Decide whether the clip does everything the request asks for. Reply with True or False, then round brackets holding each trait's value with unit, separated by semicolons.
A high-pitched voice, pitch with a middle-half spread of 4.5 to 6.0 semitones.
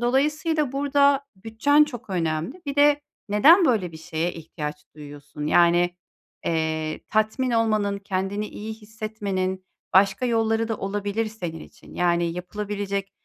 True (205 Hz; 5.1 semitones)